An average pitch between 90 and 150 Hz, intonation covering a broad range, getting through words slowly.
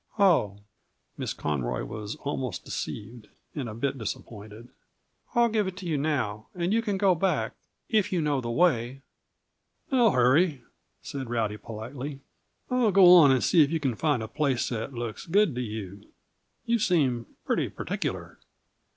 No: low, 135 Hz; wide, 7.8 semitones; average, 160 wpm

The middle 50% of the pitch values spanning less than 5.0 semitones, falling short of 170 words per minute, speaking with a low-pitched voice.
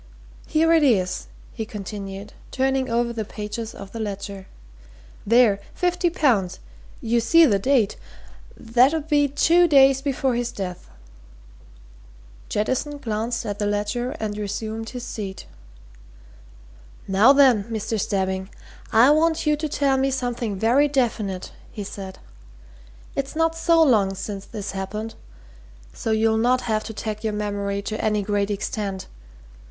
No: average, 4.6 semitones; average, 140 wpm; high, 225 Hz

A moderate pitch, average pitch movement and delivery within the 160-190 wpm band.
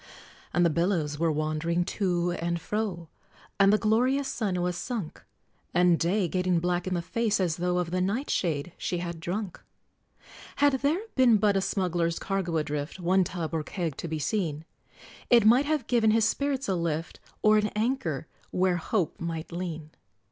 Yes: medium, 180 Hz; average, 4.1 semitones; average, 175 wpm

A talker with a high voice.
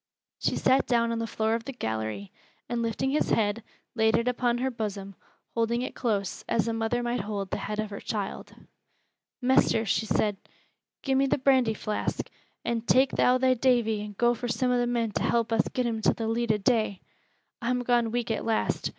Yes: high, 230 Hz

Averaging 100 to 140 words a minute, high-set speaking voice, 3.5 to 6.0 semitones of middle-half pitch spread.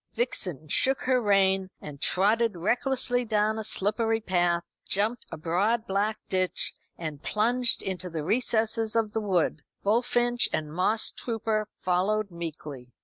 Yes: slow, 135 wpm; high, 210 Hz; average, 4.1 semitones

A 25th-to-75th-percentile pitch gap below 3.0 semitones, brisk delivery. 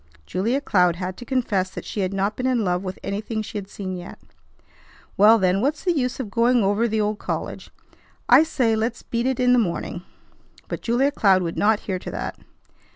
No: average, 4.4 semitones; fast, 210 wpm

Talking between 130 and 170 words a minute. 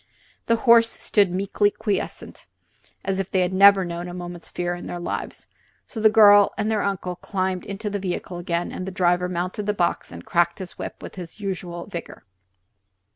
No: average, 190 wpm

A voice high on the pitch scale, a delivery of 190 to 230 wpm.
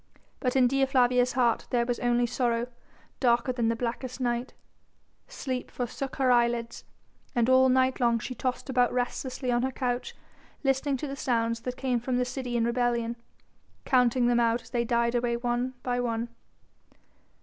No: high, 245 Hz; average, 170 wpm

